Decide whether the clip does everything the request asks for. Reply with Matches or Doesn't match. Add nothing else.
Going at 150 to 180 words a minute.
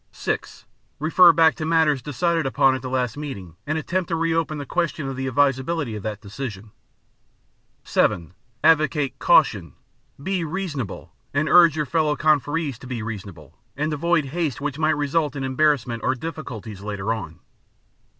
Matches